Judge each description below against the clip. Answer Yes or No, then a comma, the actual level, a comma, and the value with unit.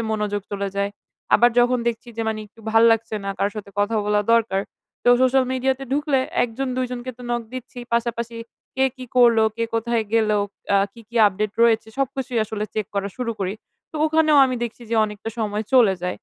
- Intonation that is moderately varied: Yes, average, 3.0 semitones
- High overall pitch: Yes, high, 230 Hz